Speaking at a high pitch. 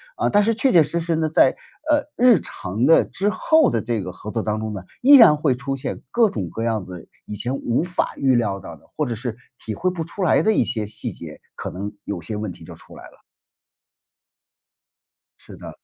No: low, 130 Hz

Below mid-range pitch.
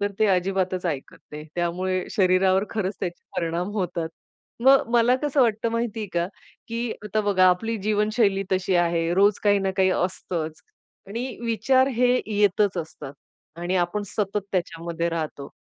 No: high, 190 Hz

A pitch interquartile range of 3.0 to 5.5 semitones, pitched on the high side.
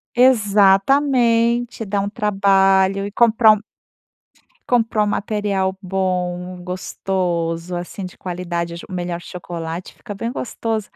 Yes: average, 3.3 semitones; high, 195 Hz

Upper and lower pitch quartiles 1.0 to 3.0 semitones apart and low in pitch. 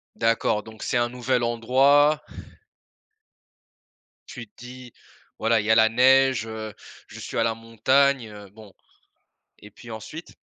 Yes: average, 2.7 semitones; low, 115 Hz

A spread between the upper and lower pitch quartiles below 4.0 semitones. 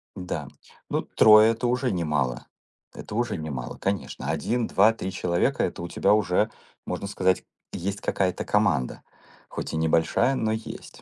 No: average, 4.3 semitones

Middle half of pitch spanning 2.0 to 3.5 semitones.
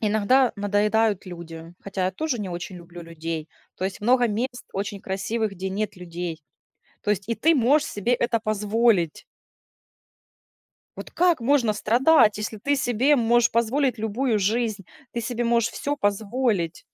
No: average, 3.9 semitones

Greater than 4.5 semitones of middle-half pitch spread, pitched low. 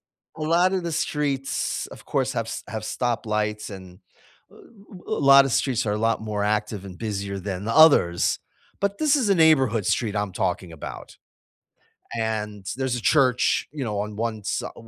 Yes: average, 5.1 semitones; low, 115 Hz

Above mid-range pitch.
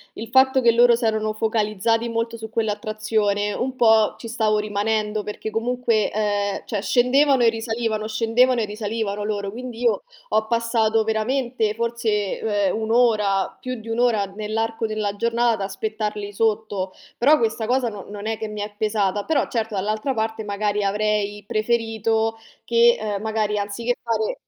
Yes: high, 220 Hz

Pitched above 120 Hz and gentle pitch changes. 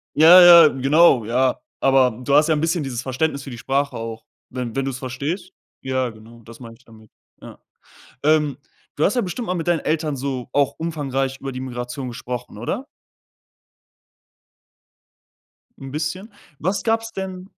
No: low, 135 Hz; average, 4.6 semitones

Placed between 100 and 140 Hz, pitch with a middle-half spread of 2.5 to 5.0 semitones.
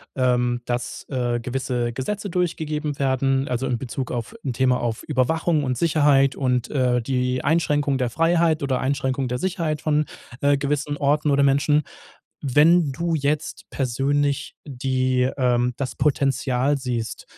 Yes: low, 135 Hz; average, 2.8 semitones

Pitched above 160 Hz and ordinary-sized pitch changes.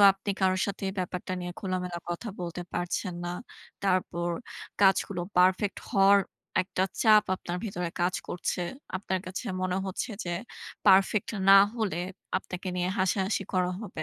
No: medium, 185 Hz; narrow, 1.6 semitones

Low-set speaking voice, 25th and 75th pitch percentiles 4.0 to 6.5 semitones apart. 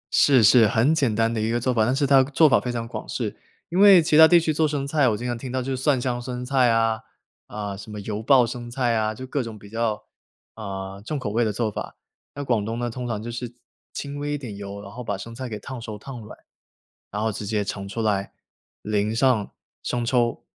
No: low, 120 Hz; average, 3.4 semitones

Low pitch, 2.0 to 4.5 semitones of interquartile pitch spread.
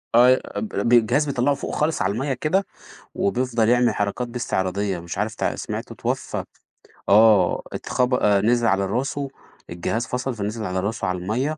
Yes: low, 115 Hz; average, 4.2 semitones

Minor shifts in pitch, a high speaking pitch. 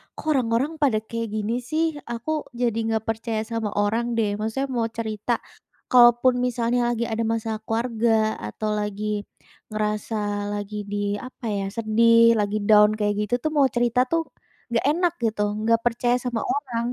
Yes: narrow, 2.0 semitones; high, 230 Hz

